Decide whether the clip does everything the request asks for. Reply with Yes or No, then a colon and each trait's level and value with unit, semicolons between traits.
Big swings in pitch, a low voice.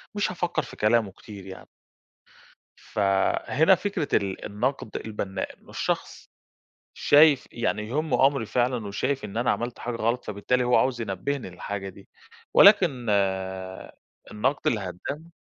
Yes: wide, 5.7 semitones; low, 120 Hz